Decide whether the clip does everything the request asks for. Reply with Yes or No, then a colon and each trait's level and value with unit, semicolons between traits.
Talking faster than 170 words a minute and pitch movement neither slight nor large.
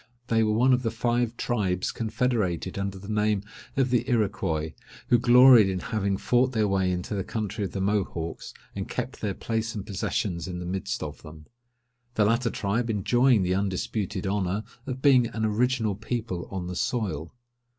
Yes: average, 180 wpm; average, 3.8 semitones